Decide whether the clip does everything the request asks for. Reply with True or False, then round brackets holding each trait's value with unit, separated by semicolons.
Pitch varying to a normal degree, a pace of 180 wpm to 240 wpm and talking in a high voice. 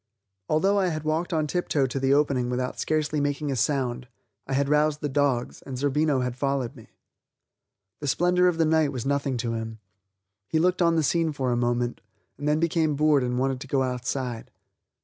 False (3.4 semitones; 200 wpm; 140 Hz)